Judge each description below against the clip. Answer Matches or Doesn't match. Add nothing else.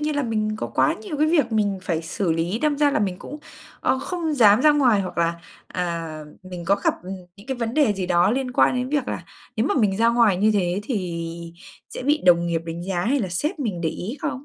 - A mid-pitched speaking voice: Doesn't match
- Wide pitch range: Matches